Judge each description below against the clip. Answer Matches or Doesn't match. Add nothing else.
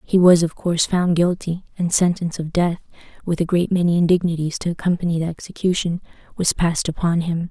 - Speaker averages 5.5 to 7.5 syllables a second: Matches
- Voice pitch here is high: Doesn't match